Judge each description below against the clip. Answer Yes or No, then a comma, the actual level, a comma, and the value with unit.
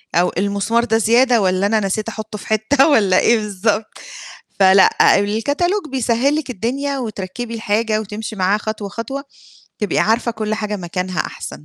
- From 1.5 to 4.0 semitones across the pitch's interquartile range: Yes, average, 2.7 semitones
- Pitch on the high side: Yes, high, 220 Hz